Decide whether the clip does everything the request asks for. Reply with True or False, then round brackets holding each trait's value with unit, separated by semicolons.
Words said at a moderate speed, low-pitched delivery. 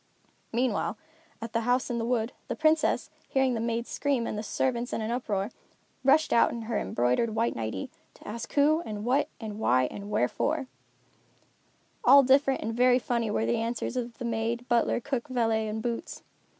False (180 wpm; 235 Hz)